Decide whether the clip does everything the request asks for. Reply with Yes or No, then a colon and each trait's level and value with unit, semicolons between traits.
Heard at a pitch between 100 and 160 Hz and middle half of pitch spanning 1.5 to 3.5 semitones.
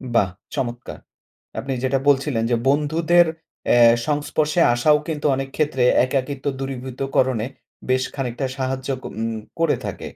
Yes: low, 135 Hz; average, 3.0 semitones